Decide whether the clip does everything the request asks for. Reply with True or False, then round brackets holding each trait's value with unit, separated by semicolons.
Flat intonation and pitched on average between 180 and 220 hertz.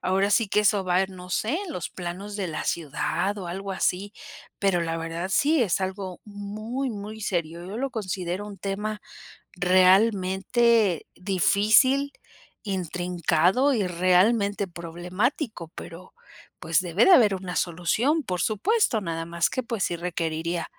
False (3.3 semitones; 190 Hz)